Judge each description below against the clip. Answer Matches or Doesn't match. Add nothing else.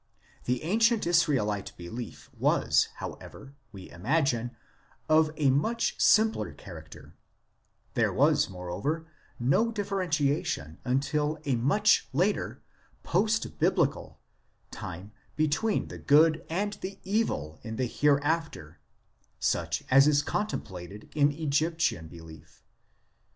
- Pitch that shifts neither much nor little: Doesn't match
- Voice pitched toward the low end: Doesn't match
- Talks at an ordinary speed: Doesn't match